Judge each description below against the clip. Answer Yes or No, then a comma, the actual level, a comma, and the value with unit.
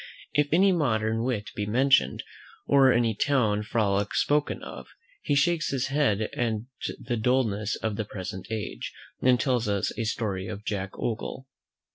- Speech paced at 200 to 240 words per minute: No, average, 155 wpm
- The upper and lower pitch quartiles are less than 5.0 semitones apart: Yes, average, 4.3 semitones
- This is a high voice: No, low, 115 Hz